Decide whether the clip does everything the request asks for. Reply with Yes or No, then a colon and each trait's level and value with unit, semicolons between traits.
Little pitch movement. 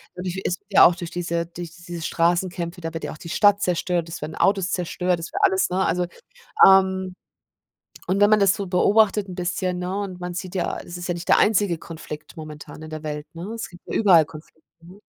Yes: narrow, 2.1 semitones